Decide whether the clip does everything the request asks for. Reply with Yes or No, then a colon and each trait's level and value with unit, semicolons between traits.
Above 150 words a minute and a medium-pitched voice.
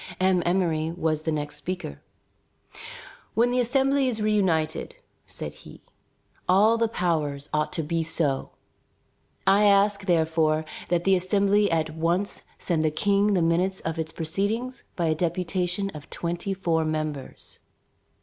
No: average, 140 wpm; medium, 175 Hz